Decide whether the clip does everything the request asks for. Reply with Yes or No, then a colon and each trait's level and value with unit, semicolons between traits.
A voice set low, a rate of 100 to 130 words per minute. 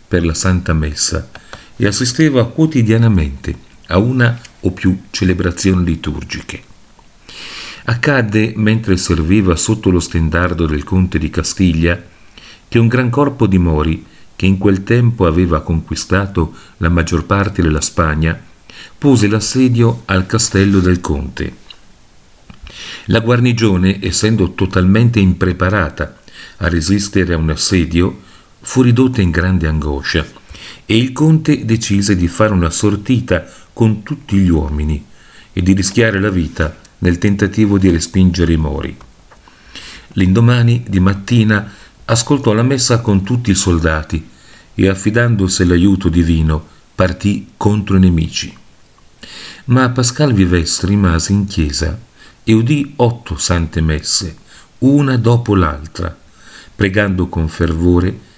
Yes: very low, 95 Hz; average, 120 wpm